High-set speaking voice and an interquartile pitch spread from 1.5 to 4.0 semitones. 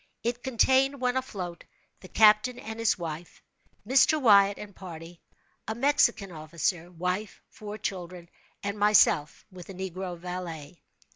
No: high, 195 Hz; average, 4.5 semitones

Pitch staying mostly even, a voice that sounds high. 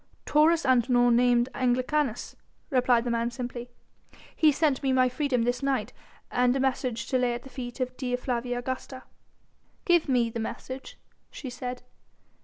Yes: narrow, 1.5 semitones; very high, 250 Hz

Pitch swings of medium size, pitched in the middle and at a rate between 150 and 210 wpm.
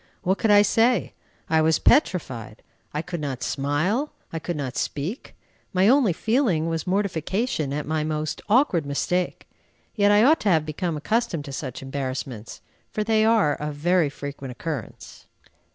No: wide, 6.1 semitones; medium, 165 Hz; average, 160 wpm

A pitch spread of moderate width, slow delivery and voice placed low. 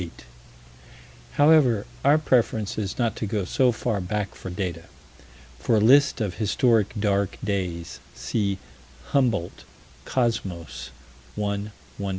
Yes: average, 3.6 semitones; slow, 120 wpm; low, 105 Hz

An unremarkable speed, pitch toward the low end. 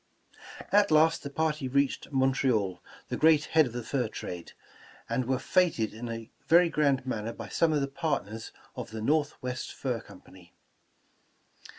Yes: average, 180 wpm; low, 130 Hz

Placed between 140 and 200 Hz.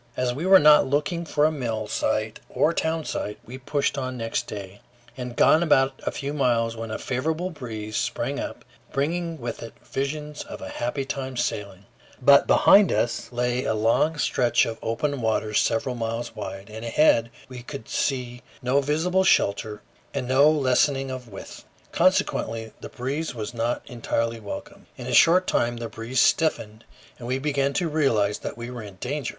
No: low, 125 Hz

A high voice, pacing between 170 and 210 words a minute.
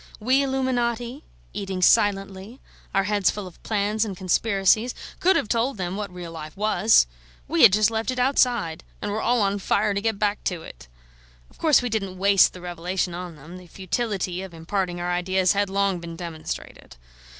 Yes: high, 200 Hz; average, 185 wpm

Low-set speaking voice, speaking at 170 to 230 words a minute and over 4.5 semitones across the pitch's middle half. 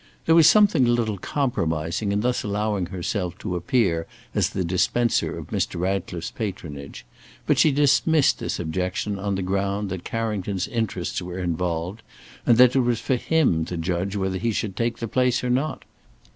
Yes: low, 100 Hz; average, 175 wpm; average, 5.0 semitones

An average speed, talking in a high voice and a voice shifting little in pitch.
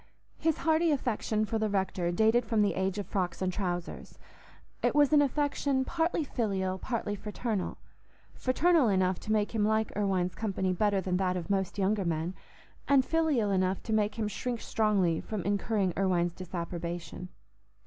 No: average, 160 wpm; high, 205 Hz; average, 3.9 semitones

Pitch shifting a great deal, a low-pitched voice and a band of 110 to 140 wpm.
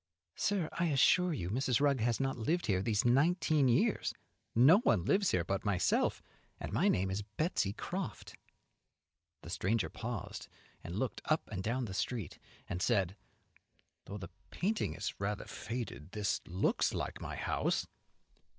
No: wide, 6.7 semitones; low, 115 Hz; average, 155 wpm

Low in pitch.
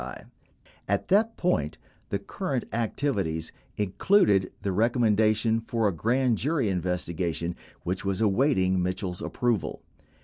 Yes: low, 105 Hz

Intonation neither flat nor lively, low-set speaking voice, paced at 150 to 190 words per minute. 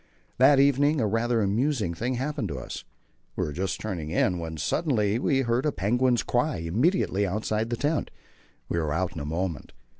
No: wide, 6.6 semitones; low, 110 Hz; average, 185 wpm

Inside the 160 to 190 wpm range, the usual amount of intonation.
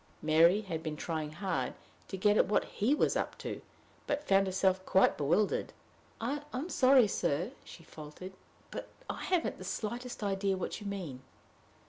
Yes: average, 165 wpm; average, 4.7 semitones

